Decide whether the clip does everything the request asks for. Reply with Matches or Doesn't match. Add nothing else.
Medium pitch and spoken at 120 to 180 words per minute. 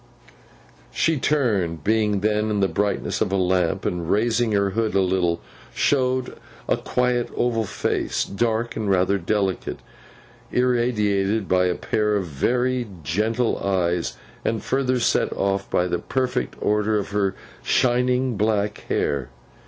Doesn't match